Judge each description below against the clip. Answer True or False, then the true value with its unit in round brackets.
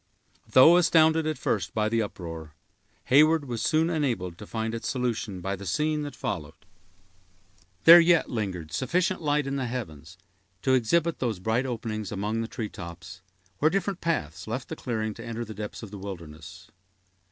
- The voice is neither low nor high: False (115 Hz)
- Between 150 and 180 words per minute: True (175 wpm)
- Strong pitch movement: True (7.5 semitones)